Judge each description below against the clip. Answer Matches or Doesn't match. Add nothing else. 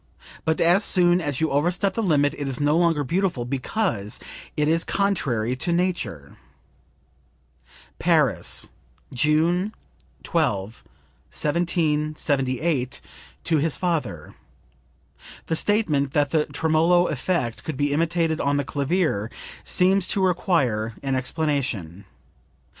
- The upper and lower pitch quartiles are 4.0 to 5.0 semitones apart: Matches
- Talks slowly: Matches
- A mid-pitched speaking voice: Matches